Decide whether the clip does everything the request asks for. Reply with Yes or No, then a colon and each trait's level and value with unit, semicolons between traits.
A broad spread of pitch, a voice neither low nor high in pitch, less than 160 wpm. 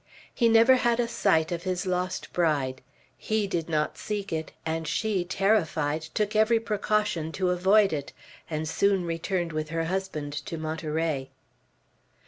No: average, 4.6 semitones; medium, 175 Hz; average, 150 wpm